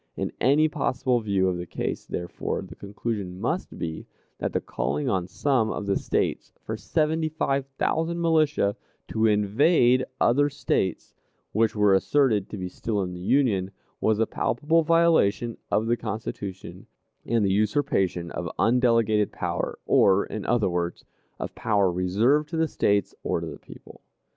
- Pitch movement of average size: No, wide, 6.1 semitones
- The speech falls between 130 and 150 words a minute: No, average, 160 wpm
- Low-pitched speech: Yes, low, 110 Hz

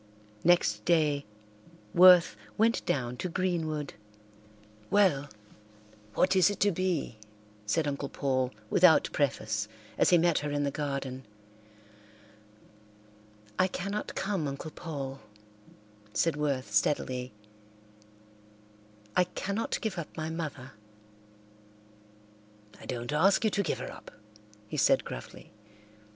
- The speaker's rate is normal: No, slow, 115 wpm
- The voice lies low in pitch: No, medium, 150 Hz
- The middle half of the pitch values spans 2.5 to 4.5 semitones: No, average, 5.1 semitones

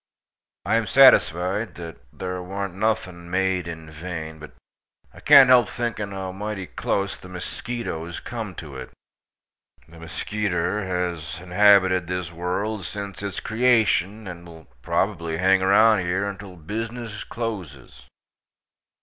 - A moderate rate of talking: No, slow, 130 wpm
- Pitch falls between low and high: No, very low, 95 Hz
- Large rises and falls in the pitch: No, average, 3.4 semitones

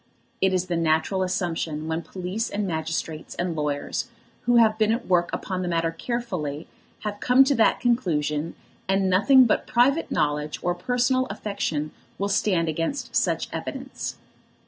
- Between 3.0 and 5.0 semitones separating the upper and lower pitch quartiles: No, wide, 5.4 semitones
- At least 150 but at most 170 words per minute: Yes, average, 160 wpm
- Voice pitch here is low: No, medium, 185 Hz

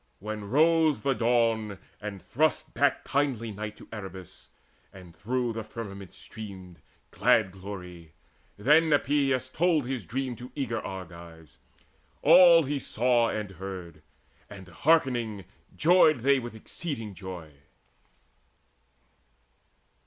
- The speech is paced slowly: Yes, slow, 115 wpm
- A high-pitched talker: No, low, 115 Hz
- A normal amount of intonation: No, wide, 6.0 semitones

